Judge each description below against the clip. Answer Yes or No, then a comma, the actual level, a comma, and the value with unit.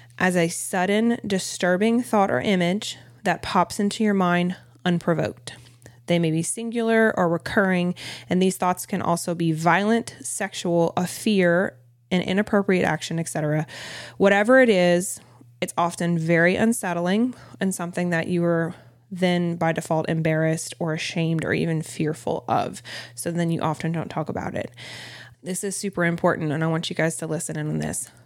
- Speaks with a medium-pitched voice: Yes, medium, 170 Hz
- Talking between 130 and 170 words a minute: Yes, average, 165 wpm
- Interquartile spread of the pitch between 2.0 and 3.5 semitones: Yes, average, 2.8 semitones